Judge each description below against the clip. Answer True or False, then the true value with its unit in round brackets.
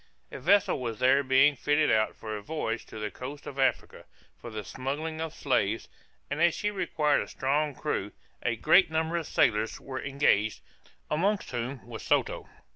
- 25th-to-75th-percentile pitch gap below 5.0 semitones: False (5.3 semitones)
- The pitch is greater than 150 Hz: False (135 Hz)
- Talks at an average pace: True (180 wpm)